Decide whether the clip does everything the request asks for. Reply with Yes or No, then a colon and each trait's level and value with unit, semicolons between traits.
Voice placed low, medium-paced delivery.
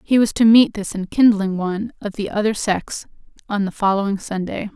No: high, 205 Hz; average, 190 wpm